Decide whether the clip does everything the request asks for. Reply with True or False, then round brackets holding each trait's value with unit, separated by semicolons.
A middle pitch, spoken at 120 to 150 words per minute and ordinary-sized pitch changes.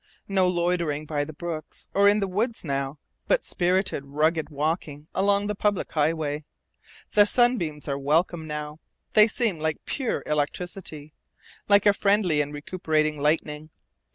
True (160 Hz; 145 wpm; 4.8 semitones)